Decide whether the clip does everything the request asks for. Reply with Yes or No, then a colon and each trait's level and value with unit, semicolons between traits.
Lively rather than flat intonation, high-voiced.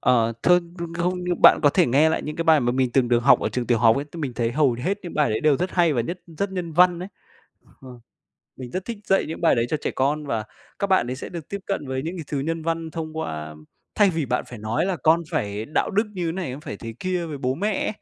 No: wide, 5.9 semitones; medium, 155 Hz